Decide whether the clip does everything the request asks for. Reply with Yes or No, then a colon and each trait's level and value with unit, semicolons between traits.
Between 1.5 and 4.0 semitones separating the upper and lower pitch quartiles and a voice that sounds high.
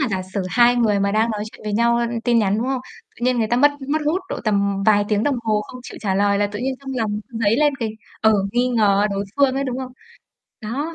Yes: average, 3.5 semitones; high, 230 Hz